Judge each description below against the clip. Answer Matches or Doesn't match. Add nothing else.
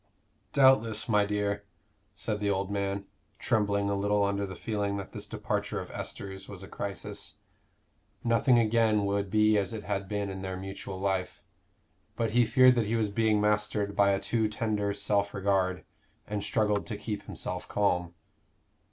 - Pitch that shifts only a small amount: Matches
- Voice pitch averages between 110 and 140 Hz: Doesn't match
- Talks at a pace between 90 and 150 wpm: Doesn't match